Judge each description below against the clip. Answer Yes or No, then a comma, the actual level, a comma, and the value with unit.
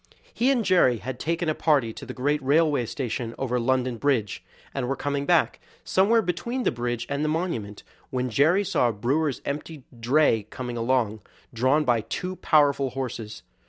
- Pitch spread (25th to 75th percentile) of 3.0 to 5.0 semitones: Yes, average, 4.4 semitones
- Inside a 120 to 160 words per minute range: No, average, 175 wpm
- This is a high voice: No, low, 135 Hz